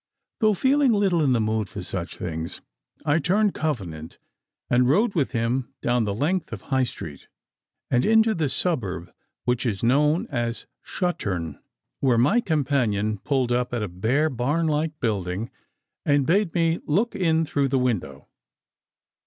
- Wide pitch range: Yes, wide, 6.9 semitones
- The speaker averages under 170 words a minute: Yes, average, 155 wpm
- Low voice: Yes, low, 130 Hz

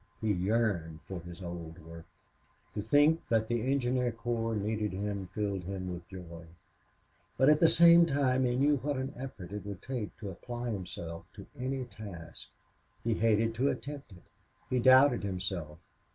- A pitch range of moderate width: No, wide, 5.7 semitones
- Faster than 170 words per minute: No, average, 165 wpm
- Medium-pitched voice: No, low, 110 Hz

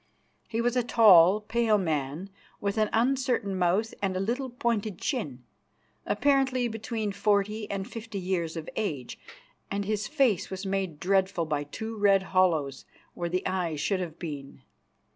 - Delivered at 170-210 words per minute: No, average, 155 wpm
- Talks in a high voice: Yes, high, 195 Hz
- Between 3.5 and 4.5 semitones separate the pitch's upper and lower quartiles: Yes, average, 4.2 semitones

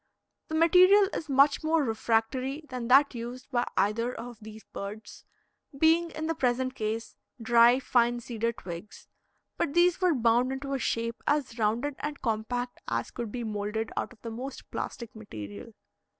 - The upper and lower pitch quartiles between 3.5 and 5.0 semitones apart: Yes, average, 3.8 semitones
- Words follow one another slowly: No, average, 165 wpm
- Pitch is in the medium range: No, high, 240 Hz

